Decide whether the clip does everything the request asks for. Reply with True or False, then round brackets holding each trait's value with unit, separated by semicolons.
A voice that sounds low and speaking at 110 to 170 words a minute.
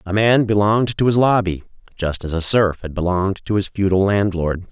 False (100 Hz; 205 wpm)